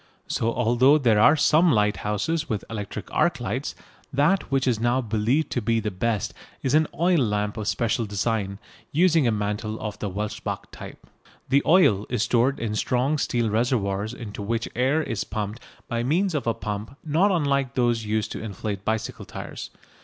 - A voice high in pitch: No, low, 115 Hz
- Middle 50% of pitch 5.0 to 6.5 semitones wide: No, average, 4.5 semitones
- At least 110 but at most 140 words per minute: No, average, 175 wpm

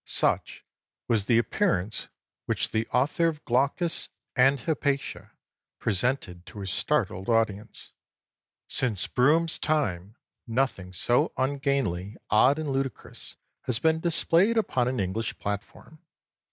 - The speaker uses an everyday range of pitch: No, wide, 5.9 semitones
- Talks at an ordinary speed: No, slow, 115 wpm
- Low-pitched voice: Yes, low, 125 Hz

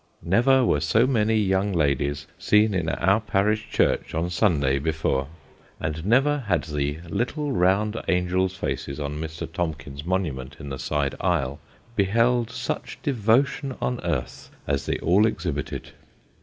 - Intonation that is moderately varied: No, wide, 6.6 semitones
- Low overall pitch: Yes, very low, 90 Hz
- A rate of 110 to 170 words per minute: Yes, average, 140 wpm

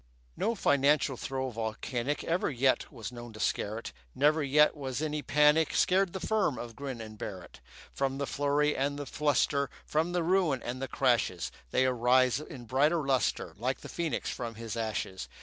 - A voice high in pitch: No, low, 135 Hz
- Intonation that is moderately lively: Yes, average, 3.9 semitones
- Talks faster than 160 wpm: Yes, average, 180 wpm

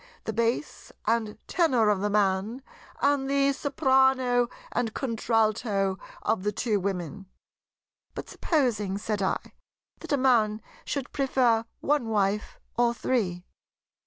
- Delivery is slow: Yes, slow, 125 wpm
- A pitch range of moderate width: Yes, average, 4.2 semitones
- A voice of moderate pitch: No, high, 230 Hz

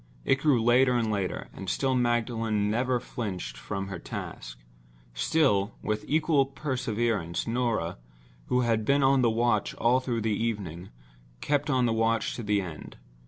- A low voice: Yes, low, 115 Hz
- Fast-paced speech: No, average, 155 wpm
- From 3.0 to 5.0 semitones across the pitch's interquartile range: Yes, average, 4.1 semitones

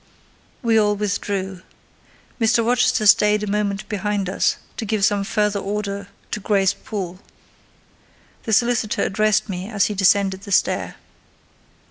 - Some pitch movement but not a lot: No, narrow, 1.4 semitones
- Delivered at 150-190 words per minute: No, slow, 135 wpm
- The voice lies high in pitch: Yes, high, 205 Hz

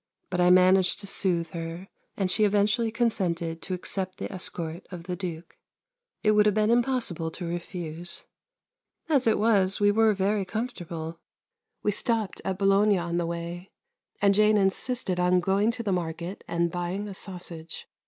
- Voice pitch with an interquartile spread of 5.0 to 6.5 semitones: No, average, 3.3 semitones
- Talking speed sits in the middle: Yes, average, 165 wpm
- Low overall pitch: No, high, 190 Hz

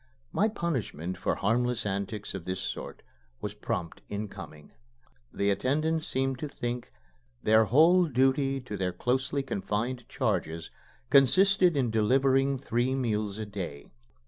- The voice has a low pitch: Yes, low, 120 Hz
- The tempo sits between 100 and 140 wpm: Yes, slow, 135 wpm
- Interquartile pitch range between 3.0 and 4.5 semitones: No, average, 5.1 semitones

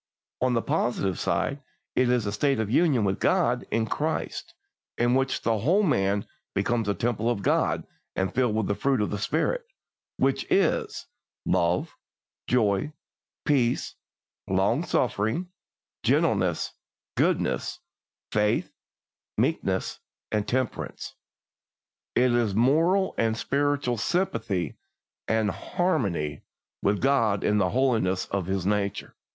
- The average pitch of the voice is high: No, low, 115 Hz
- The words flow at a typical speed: No, slow, 125 wpm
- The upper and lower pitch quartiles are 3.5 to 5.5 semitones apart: Yes, average, 5.0 semitones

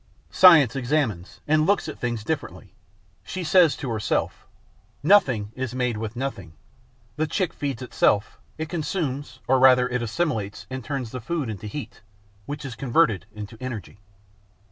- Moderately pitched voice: No, low, 130 Hz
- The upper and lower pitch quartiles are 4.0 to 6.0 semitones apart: Yes, wide, 5.4 semitones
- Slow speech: No, average, 150 wpm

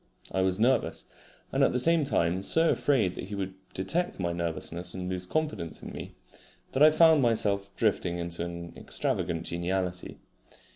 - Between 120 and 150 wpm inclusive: No, average, 165 wpm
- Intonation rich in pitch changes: Yes, wide, 6.9 semitones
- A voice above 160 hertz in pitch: No, very low, 95 Hz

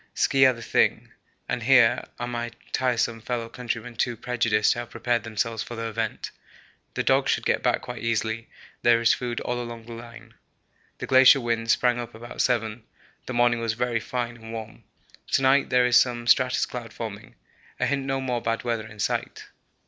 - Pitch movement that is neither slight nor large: No, narrow, 1.3 semitones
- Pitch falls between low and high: No, low, 120 Hz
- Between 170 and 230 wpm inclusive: Yes, average, 195 wpm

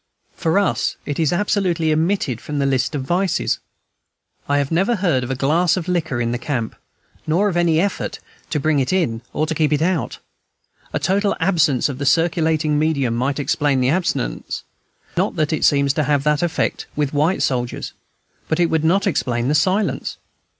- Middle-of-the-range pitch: Yes, medium, 155 Hz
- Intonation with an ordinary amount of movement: Yes, average, 3.9 semitones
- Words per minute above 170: Yes, average, 190 wpm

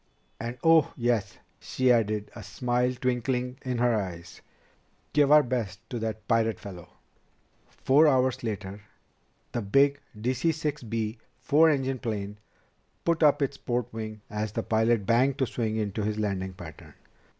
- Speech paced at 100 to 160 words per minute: Yes, average, 150 wpm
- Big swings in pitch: No, average, 3.5 semitones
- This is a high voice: No, low, 115 Hz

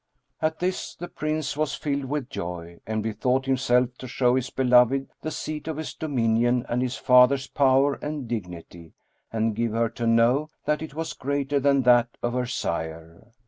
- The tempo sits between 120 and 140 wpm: No, average, 180 wpm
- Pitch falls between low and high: No, low, 125 Hz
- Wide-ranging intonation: No, average, 3.5 semitones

